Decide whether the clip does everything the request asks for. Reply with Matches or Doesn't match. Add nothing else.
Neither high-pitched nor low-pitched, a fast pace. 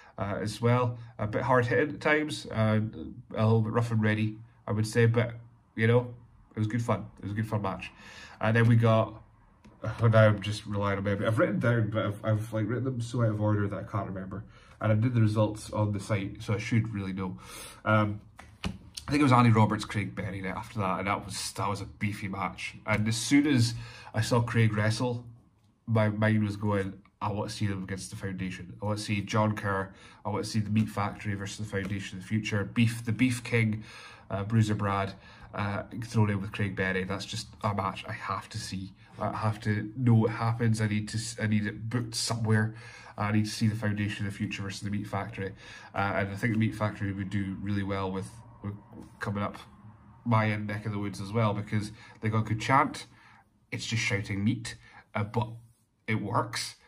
Doesn't match